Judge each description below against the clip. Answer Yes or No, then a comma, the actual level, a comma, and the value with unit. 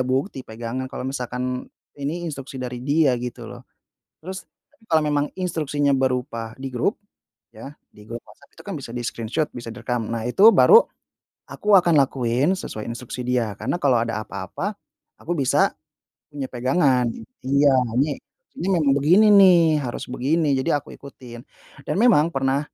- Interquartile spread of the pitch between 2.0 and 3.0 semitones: No, average, 4.1 semitones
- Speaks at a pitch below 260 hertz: Yes, low, 135 Hz